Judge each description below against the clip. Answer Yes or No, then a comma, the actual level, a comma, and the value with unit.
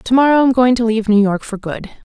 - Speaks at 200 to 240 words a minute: No, fast, 285 wpm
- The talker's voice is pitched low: No, high, 230 Hz